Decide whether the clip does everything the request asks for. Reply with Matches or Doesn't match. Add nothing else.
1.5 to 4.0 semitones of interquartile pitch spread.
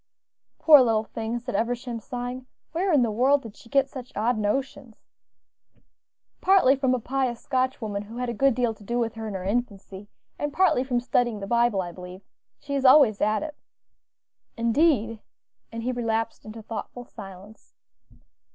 Matches